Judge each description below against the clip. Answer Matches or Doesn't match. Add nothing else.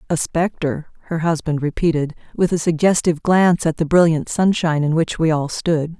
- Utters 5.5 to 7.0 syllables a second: Doesn't match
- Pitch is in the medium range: Matches